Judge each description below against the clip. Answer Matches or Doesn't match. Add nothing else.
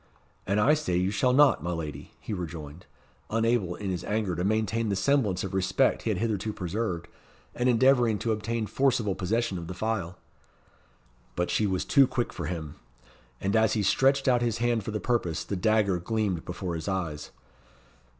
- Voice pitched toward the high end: Doesn't match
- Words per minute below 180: Doesn't match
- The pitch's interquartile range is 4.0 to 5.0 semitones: Matches